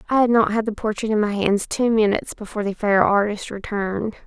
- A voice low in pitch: No, high, 210 Hz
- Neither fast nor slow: No, fast, 225 wpm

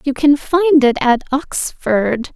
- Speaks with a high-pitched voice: Yes, very high, 275 Hz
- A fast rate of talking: No, average, 155 wpm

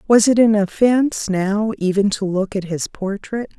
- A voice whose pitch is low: No, high, 205 Hz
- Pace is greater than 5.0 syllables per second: No, 4.4 syllables/s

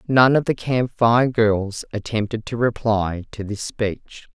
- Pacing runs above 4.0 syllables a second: No, 3.7 syllables/s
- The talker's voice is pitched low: Yes, low, 115 Hz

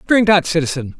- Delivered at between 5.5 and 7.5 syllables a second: Yes, 5.9 syllables/s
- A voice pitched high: No, medium, 170 Hz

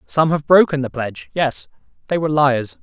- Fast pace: No, average, 190 wpm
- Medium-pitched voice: Yes, medium, 145 Hz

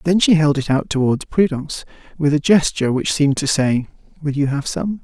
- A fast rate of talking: Yes, fast, 215 wpm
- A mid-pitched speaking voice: Yes, medium, 150 Hz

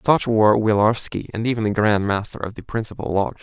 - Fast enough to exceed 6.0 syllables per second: Yes, 6.2 syllables/s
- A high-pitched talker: No, low, 110 Hz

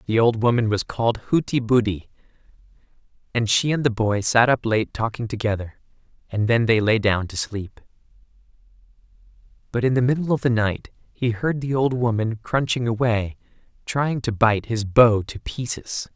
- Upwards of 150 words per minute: Yes, average, 165 wpm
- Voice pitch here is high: No, low, 115 Hz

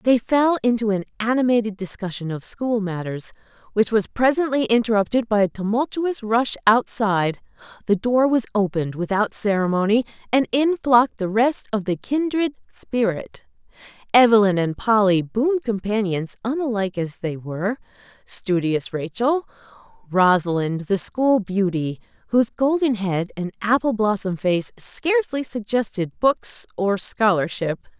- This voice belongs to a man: No, female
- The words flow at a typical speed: No, slow, 125 wpm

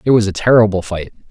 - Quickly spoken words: Yes, fast, 230 wpm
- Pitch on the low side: Yes, low, 100 Hz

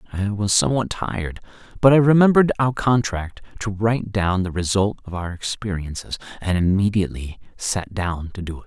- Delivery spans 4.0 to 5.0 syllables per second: No, 5.5 syllables/s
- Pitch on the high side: No, low, 100 Hz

